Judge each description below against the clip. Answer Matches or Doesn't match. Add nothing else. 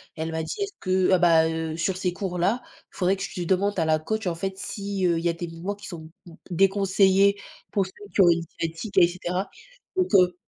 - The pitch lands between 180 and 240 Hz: Matches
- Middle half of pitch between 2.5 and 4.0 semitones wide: Matches